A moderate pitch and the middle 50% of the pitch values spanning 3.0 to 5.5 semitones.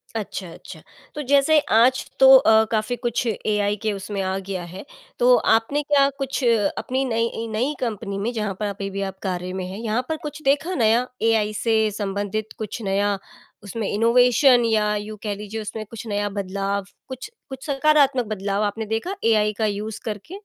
No: high, 220 Hz; average, 3.6 semitones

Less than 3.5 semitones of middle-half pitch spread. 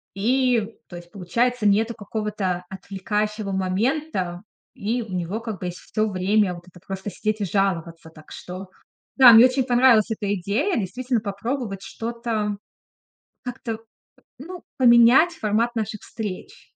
No: average, 3.8 semitones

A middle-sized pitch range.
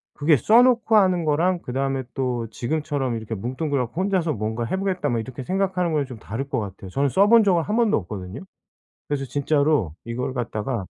No: wide, 7.1 semitones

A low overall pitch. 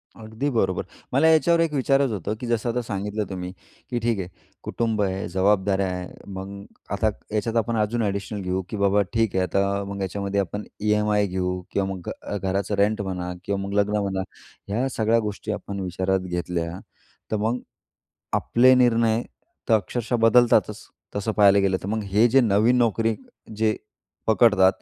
Yes: low, 105 Hz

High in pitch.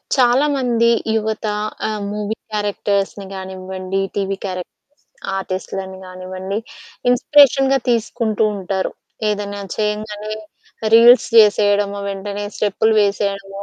Yes: high, 205 Hz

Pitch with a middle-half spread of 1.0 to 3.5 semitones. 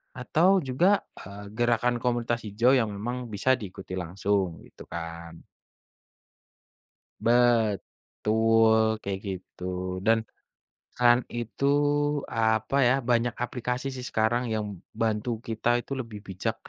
Yes: average, 3.1 semitones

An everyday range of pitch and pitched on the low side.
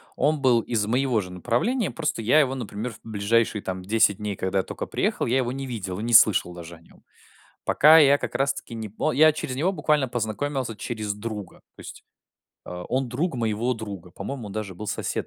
Yes: average, 4.5 semitones; low, 115 Hz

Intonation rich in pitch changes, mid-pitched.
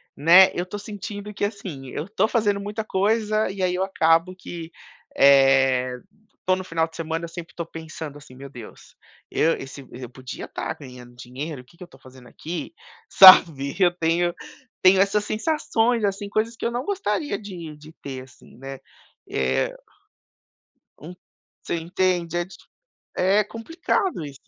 Yes: wide, 6.4 semitones; medium, 175 Hz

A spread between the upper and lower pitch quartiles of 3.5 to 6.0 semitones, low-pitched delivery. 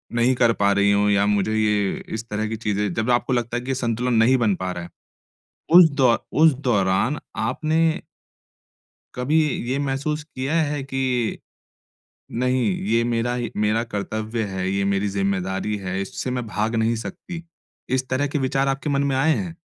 Yes: average, 4.3 semitones; low, 120 Hz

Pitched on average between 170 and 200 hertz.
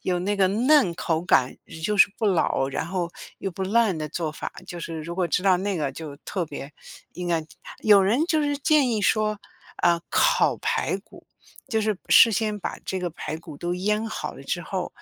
Yes: medium, 185 Hz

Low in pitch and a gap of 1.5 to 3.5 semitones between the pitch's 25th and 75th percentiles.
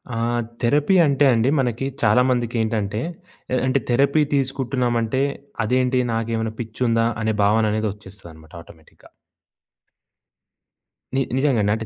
Yes: low, 115 Hz; average, 2.8 semitones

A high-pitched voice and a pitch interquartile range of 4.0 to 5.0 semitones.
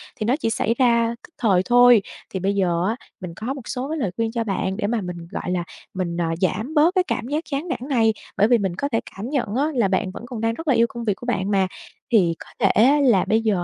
Yes: high, 225 Hz; average, 4.5 semitones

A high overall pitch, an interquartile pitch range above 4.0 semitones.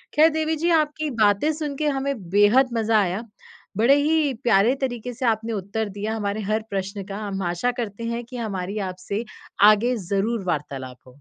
Yes: high, 220 Hz; average, 4.6 semitones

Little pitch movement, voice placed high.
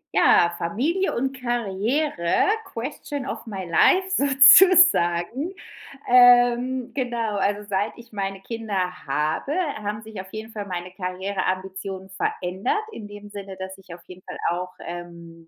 No: average, 4.8 semitones; high, 205 Hz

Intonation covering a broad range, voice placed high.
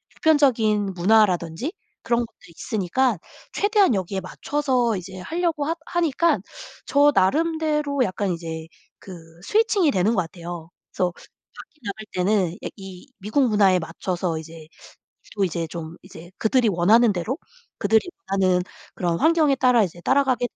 Yes: wide, 7.3 semitones; high, 210 Hz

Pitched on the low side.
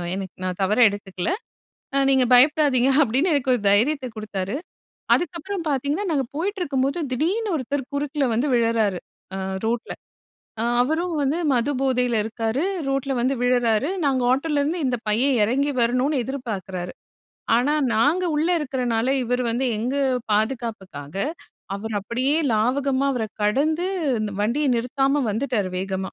No: very high, 255 Hz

